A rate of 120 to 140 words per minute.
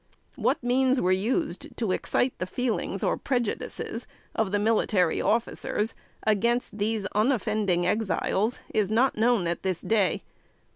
Yes: slow, 135 wpm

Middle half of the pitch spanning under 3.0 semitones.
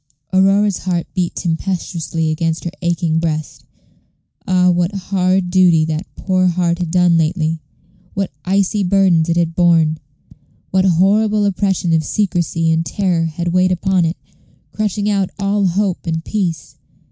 Yes: narrow, 2.6 semitones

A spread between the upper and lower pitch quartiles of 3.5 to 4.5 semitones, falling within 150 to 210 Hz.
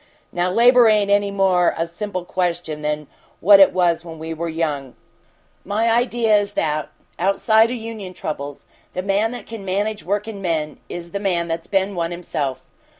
Yes: average, 3.8 semitones; medium, 185 Hz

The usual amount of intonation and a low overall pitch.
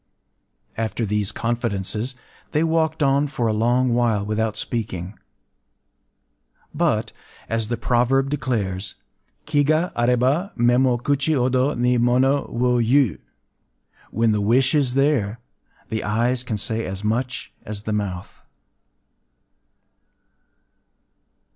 Yes: average, 3.6 semitones; low, 120 Hz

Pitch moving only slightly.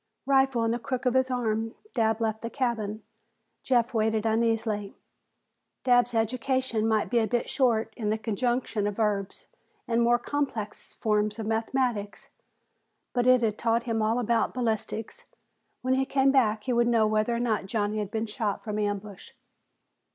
Yes: narrow, 2.2 semitones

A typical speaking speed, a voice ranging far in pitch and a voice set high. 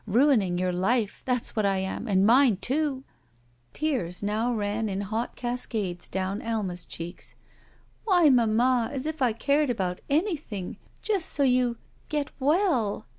Yes: average, 155 wpm; wide, 5.7 semitones; high, 230 Hz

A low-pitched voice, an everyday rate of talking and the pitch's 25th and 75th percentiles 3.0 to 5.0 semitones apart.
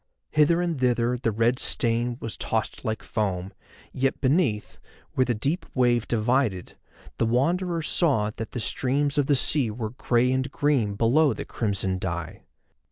Yes: low, 120 Hz; average, 160 wpm; average, 4.1 semitones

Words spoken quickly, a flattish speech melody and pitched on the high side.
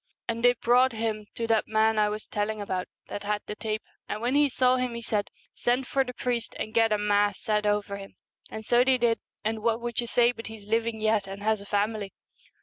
Yes: fast, 240 wpm; narrow, 2.2 semitones; high, 220 Hz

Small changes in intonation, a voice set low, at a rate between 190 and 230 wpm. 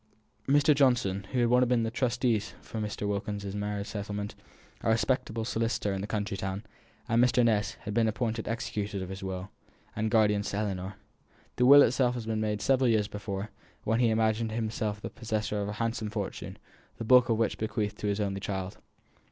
Yes: narrow, 2.2 semitones; low, 110 Hz; average, 200 wpm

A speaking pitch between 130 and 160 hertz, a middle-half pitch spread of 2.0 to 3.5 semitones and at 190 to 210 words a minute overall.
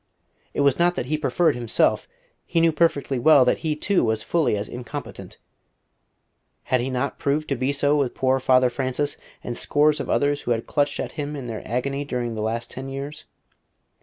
Yes: medium, 140 Hz; average, 3.1 semitones; average, 195 wpm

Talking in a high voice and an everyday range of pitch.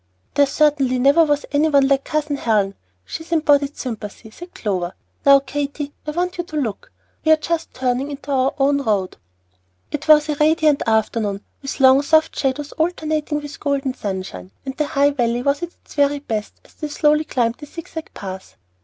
Yes: very high, 280 Hz; average, 3.3 semitones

